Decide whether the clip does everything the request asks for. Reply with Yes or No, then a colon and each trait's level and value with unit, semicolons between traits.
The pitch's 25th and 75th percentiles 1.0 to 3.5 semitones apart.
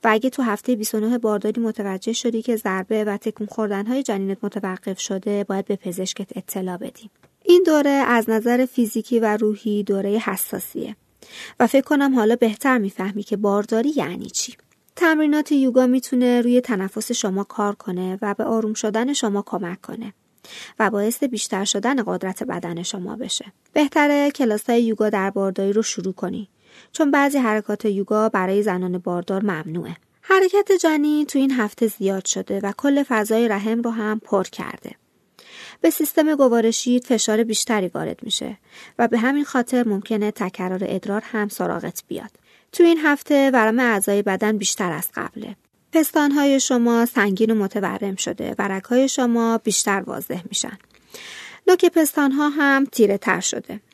No: average, 4.1 semitones